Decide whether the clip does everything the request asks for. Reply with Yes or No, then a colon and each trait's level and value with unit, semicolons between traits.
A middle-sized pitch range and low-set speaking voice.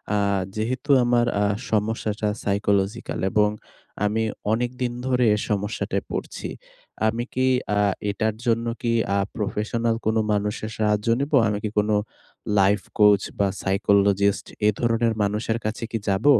No: narrow, 2.2 semitones; low, 110 Hz